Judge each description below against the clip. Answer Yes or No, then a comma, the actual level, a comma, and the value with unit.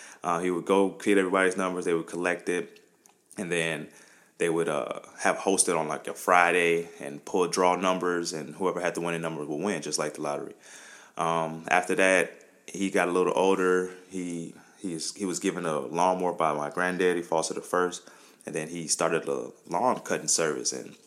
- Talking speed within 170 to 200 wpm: Yes, average, 190 wpm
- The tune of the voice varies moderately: No, narrow, 1.8 semitones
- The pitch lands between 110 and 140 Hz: No, very low, 90 Hz